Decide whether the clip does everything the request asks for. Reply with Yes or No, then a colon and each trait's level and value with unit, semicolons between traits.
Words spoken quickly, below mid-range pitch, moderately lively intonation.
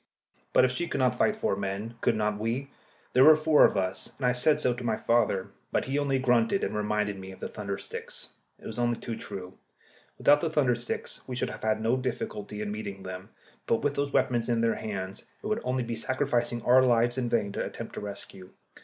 Yes: fast, 235 wpm; low, 120 Hz; average, 3.7 semitones